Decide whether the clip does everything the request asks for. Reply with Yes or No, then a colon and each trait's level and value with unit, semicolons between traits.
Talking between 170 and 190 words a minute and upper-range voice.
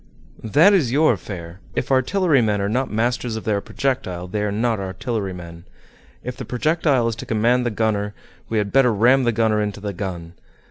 No: average, 185 wpm; low, 110 Hz